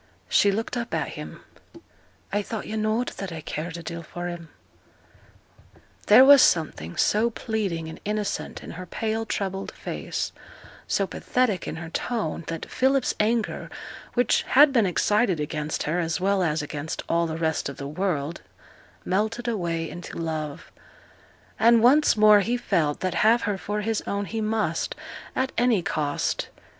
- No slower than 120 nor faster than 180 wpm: Yes, average, 160 wpm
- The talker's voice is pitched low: No, high, 195 Hz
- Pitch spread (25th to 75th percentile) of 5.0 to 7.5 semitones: Yes, average, 5.3 semitones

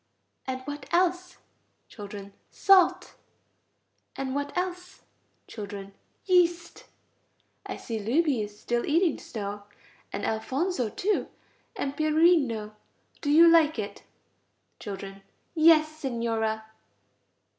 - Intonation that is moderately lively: No, wide, 7.5 semitones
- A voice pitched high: Yes, very high, 275 Hz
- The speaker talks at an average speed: No, slow, 100 wpm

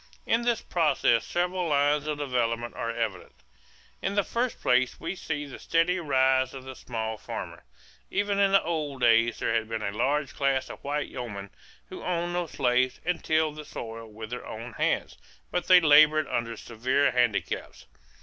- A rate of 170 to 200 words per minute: Yes, average, 180 wpm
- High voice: No, medium, 140 Hz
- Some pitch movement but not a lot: No, wide, 5.9 semitones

